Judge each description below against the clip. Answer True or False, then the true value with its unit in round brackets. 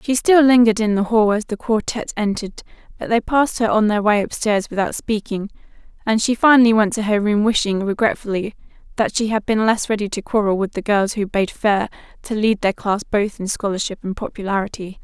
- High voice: True (215 Hz)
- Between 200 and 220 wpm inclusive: True (205 wpm)